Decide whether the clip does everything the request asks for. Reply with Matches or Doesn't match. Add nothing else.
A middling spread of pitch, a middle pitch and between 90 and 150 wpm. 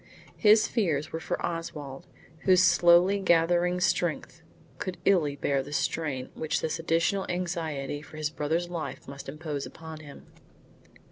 Matches